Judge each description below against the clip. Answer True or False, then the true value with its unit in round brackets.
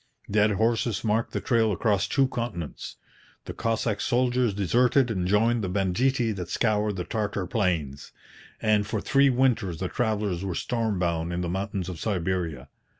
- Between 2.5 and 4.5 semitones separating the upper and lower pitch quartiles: True (4.1 semitones)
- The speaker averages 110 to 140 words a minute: False (160 wpm)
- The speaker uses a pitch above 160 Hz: False (105 Hz)